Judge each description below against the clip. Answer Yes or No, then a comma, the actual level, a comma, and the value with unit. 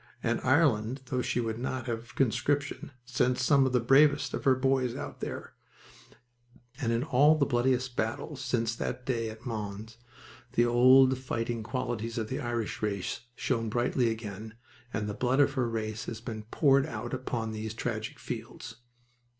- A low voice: Yes, low, 120 Hz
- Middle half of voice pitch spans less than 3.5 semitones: Yes, average, 2.7 semitones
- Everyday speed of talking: Yes, average, 165 wpm